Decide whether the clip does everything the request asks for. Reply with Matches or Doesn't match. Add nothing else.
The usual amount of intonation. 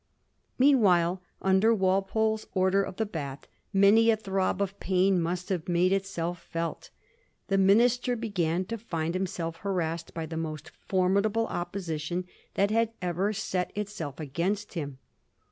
Matches